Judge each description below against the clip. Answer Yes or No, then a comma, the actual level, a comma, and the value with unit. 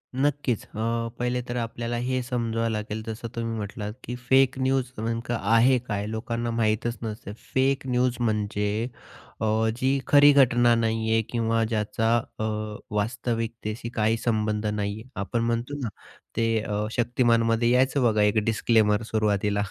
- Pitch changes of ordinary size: No, narrow, 2.1 semitones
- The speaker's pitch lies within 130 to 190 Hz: No, low, 115 Hz